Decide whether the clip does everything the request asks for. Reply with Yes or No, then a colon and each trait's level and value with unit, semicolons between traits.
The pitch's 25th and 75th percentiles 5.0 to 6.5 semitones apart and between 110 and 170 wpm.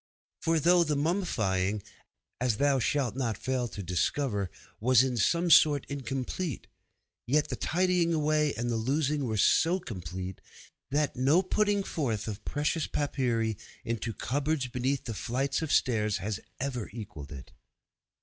Yes: wide, 5.4 semitones; average, 140 wpm